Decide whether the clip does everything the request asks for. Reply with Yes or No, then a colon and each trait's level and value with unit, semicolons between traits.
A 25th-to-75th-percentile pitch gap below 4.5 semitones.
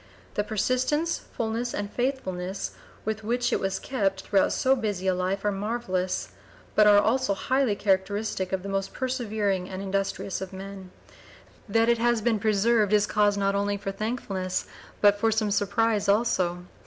Yes: average, 2.7 semitones